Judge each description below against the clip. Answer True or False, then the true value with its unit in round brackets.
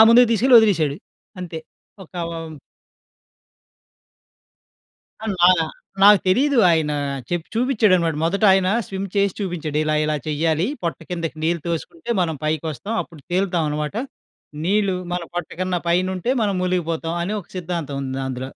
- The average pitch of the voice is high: False (175 Hz)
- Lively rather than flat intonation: False (3.7 semitones)